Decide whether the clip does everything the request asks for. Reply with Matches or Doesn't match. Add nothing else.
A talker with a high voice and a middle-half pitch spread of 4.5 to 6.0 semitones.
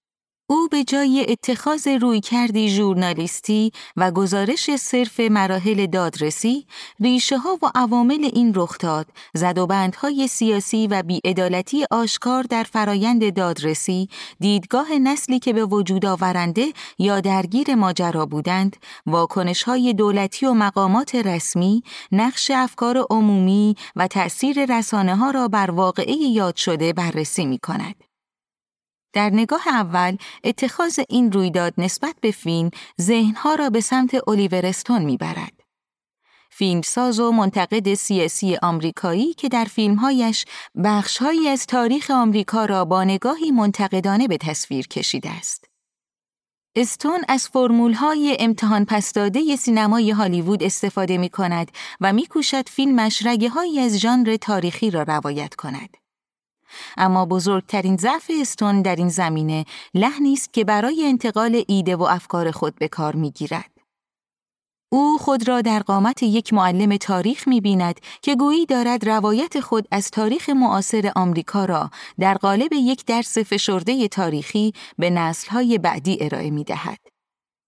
Matches